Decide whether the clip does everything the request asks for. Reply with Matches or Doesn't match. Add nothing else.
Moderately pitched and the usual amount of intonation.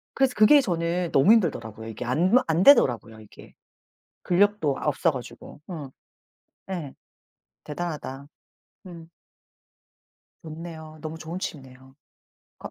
Matches